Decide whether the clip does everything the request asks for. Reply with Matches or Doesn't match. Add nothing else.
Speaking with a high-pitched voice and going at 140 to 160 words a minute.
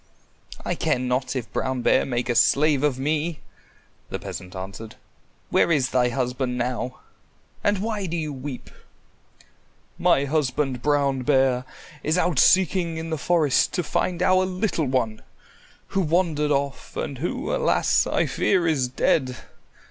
Doesn't match